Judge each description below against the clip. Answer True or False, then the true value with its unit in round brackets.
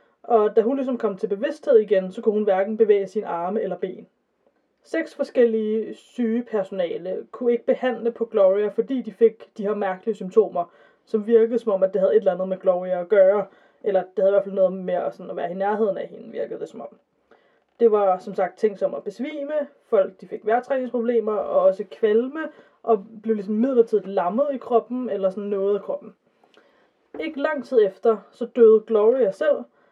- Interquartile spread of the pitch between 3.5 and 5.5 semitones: True (3.8 semitones)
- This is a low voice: False (220 Hz)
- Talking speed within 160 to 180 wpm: False (205 wpm)